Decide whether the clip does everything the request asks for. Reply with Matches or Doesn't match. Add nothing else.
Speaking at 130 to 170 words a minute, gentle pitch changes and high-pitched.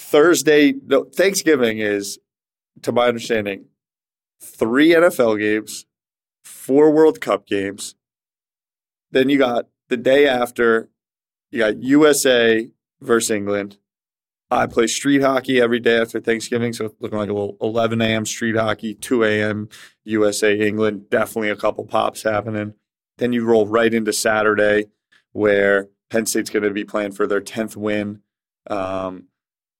Doesn't match